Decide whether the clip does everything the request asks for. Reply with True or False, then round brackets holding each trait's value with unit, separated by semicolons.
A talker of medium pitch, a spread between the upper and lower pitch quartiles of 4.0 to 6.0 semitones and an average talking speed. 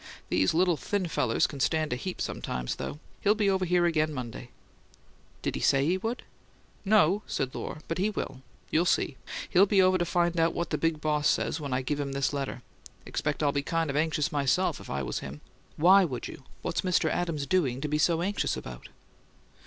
False (155 Hz; 4.5 semitones; 210 wpm)